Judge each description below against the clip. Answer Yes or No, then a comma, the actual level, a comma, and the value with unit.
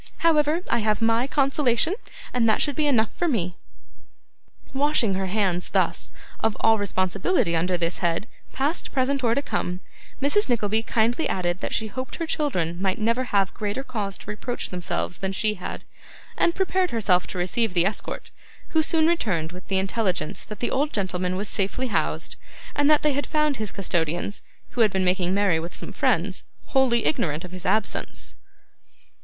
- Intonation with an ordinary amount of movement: No, wide, 6.3 semitones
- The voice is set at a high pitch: Yes, high, 215 Hz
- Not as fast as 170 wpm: No, average, 175 wpm